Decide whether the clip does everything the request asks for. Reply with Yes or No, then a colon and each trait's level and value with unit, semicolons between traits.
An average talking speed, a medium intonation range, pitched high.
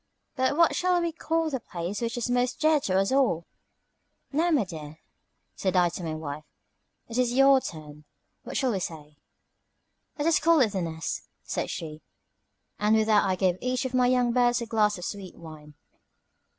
No: average, 190 wpm; wide, 7.3 semitones; high, 220 Hz